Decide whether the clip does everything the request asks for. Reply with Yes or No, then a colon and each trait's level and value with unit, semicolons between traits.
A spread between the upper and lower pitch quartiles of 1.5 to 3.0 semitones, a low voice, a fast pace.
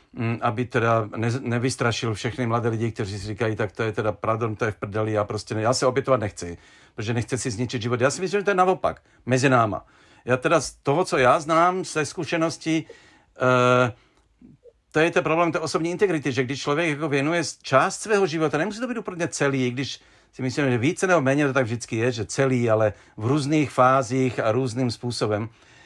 No: average, 5.1 semitones; low, 130 Hz; fast, 210 wpm